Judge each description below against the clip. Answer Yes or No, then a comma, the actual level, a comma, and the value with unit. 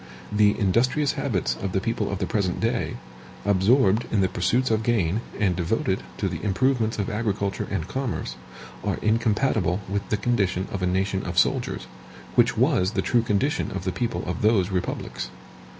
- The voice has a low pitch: Yes, low, 105 Hz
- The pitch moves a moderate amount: Yes, average, 3.5 semitones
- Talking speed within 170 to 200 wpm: Yes, average, 175 wpm